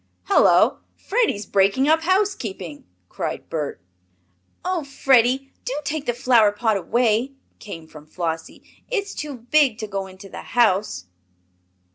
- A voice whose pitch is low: No, high, 235 Hz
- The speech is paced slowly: Yes, slow, 130 wpm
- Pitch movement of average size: No, wide, 6.7 semitones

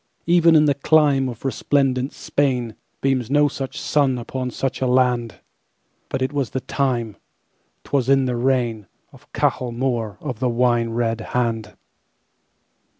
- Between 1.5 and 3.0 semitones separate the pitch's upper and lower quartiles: Yes, narrow, 2.5 semitones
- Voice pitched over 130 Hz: No, low, 125 Hz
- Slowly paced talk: Yes, slow, 130 wpm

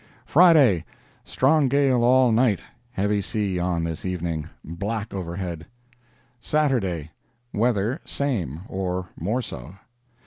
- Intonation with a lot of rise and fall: Yes, wide, 6.3 semitones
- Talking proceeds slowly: Yes, slow, 95 wpm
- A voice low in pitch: Yes, low, 100 Hz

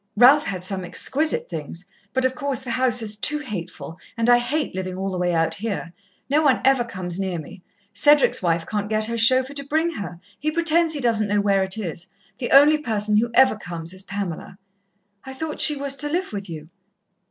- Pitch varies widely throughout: Yes, wide, 6.7 semitones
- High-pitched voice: Yes, high, 220 Hz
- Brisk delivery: Yes, fast, 210 wpm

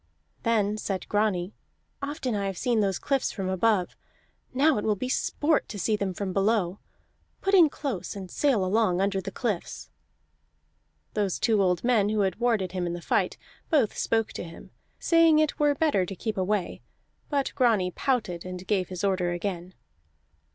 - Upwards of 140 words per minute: Yes, average, 175 wpm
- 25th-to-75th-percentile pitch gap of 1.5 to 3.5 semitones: No, average, 4.7 semitones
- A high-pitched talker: Yes, high, 205 Hz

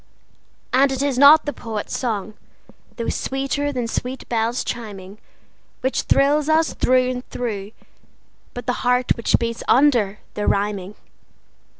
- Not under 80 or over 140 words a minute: Yes, slow, 135 wpm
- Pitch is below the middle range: No, high, 245 Hz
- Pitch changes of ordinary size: Yes, average, 3.8 semitones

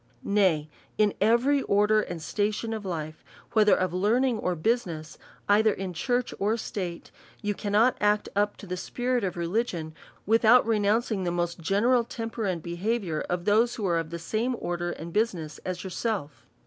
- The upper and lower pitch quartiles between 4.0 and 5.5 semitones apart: Yes, average, 4.5 semitones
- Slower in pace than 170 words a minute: No, average, 175 wpm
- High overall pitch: Yes, high, 205 Hz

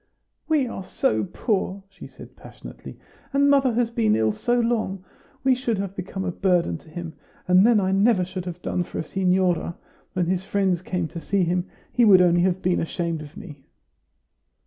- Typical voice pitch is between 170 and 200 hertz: Yes, medium, 185 Hz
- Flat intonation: No, average, 3.5 semitones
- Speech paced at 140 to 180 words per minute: No, average, 190 wpm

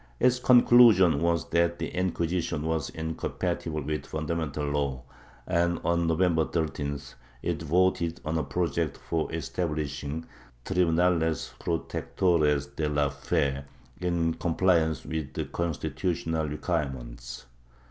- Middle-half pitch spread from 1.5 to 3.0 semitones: Yes, average, 2.7 semitones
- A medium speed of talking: No, slow, 115 wpm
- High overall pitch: No, very low, 80 Hz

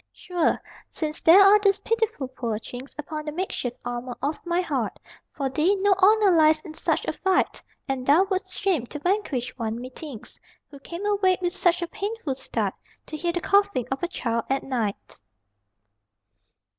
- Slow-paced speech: No, average, 180 wpm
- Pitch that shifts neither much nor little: No, wide, 6.4 semitones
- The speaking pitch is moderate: No, very high, 325 Hz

